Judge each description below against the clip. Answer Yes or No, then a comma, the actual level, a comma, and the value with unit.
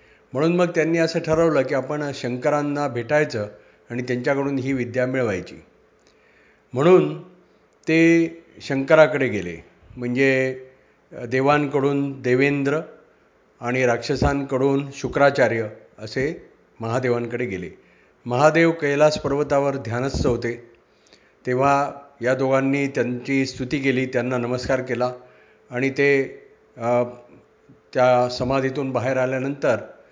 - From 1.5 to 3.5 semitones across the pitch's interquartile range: Yes, narrow, 2.6 semitones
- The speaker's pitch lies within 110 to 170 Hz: Yes, low, 135 Hz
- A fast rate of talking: No, average, 95 wpm